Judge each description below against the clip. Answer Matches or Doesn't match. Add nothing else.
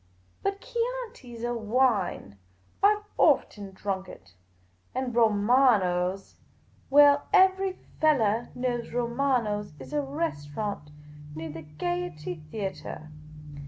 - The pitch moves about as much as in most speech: Doesn't match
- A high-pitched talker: Matches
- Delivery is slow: Matches